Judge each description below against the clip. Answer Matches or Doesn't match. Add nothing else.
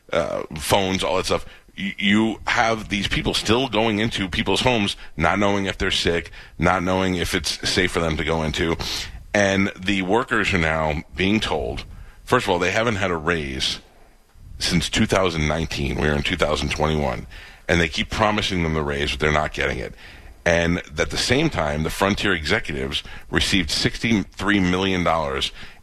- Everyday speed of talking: Matches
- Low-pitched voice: Matches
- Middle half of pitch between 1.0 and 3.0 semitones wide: Doesn't match